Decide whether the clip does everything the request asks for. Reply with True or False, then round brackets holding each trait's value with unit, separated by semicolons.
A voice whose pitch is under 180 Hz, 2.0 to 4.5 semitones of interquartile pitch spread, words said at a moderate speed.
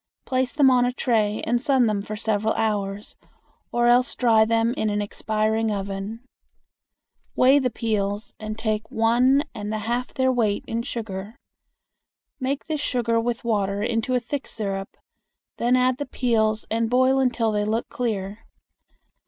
False (225 Hz; 2.7 semitones; 160 wpm)